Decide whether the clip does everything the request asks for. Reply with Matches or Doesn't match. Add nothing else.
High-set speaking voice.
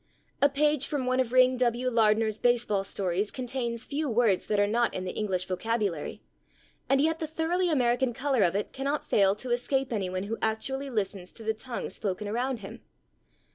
Matches